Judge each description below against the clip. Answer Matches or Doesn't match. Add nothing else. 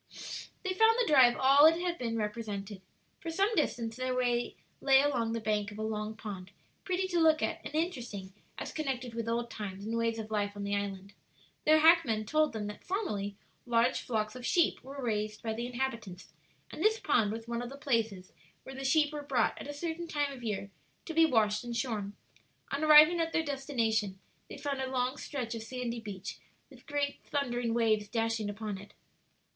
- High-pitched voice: Matches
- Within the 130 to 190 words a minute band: Doesn't match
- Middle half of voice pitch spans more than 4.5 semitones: Matches